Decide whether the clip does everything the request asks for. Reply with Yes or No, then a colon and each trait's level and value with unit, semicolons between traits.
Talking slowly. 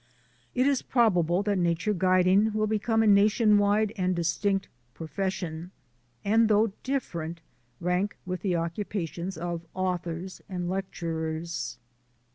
Yes: slow, 120 wpm